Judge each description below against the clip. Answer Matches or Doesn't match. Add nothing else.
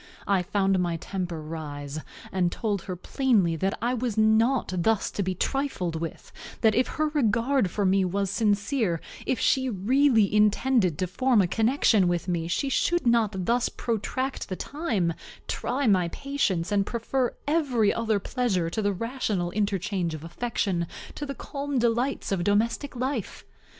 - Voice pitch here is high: Matches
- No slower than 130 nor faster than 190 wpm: Matches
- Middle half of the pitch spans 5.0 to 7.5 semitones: Matches